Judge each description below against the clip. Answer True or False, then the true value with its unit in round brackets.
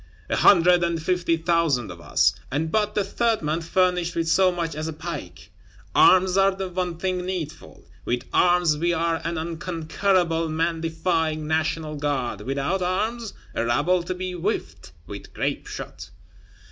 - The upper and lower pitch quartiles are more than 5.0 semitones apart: False (2.5 semitones)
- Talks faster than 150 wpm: True (160 wpm)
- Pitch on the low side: False (170 Hz)